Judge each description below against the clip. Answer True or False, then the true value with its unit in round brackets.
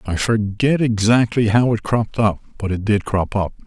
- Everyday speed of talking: True (195 wpm)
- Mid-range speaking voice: False (110 Hz)